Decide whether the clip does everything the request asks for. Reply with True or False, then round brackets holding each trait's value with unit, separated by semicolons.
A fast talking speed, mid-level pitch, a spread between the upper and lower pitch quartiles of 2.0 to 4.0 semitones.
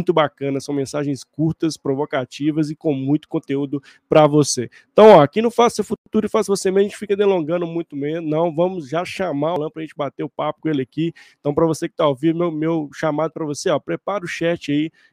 True (235 wpm; 160 Hz; 3.0 semitones)